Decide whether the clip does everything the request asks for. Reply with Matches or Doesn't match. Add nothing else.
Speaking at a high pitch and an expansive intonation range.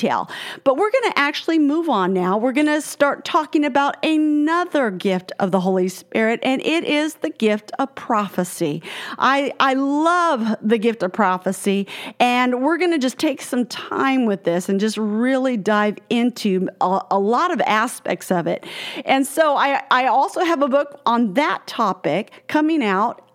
Matches